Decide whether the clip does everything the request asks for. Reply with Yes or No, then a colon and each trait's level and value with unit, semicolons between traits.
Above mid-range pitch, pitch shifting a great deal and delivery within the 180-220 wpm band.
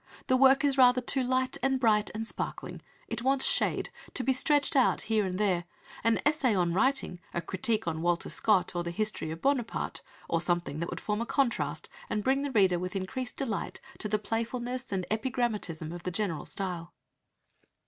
Yes: high, 220 Hz; wide, 6.1 semitones; average, 190 wpm